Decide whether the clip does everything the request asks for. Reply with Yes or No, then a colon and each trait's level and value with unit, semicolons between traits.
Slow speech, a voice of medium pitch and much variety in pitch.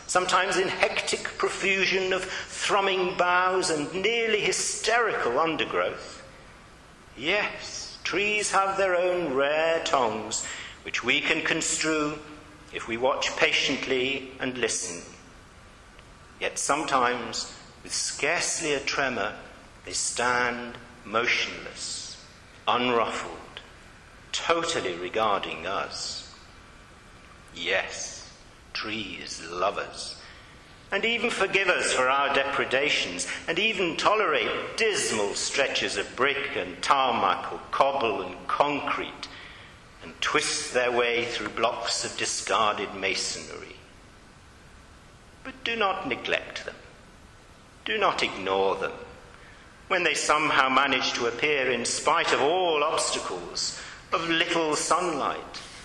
Yes: slow, 105 wpm; medium, 170 Hz; wide, 5.8 semitones